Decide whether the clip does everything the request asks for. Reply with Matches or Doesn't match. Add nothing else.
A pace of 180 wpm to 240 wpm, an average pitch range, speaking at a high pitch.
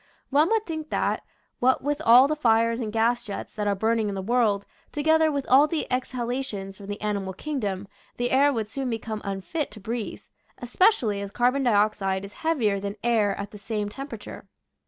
Matches